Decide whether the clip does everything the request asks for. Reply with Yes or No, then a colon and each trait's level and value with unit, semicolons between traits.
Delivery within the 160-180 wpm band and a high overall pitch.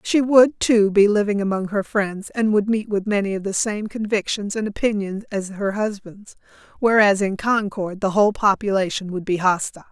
No: average, 190 wpm; high, 205 Hz